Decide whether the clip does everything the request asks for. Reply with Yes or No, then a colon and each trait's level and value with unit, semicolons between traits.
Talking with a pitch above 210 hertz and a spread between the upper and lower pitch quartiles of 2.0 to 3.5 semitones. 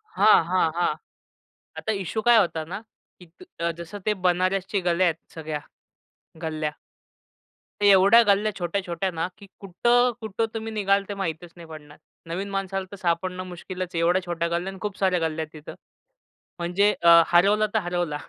No: medium, 185 Hz; average, 3.0 semitones